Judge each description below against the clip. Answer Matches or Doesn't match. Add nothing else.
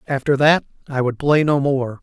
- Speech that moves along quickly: Matches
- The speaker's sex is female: Doesn't match